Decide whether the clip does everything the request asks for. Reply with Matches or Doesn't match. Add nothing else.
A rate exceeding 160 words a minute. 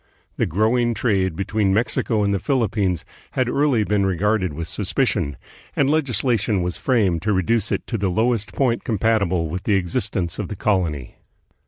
Matches